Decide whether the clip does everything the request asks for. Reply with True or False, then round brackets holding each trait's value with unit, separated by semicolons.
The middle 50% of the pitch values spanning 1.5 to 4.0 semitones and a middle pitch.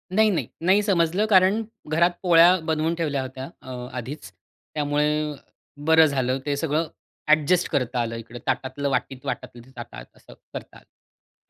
False (4.4 semitones; 150 Hz)